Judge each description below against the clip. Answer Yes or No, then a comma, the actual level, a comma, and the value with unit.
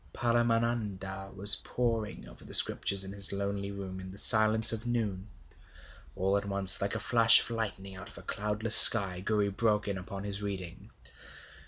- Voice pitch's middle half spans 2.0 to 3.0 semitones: Yes, narrow, 2.4 semitones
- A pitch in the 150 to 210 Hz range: No, low, 100 Hz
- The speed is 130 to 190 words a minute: Yes, average, 175 wpm